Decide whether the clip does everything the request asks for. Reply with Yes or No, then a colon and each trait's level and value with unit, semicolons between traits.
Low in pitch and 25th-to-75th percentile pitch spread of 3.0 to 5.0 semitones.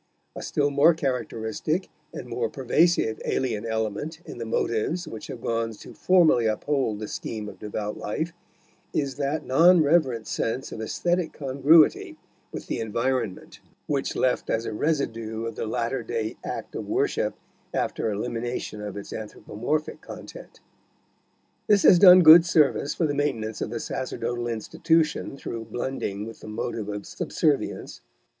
No: low, 120 Hz; wide, 5.5 semitones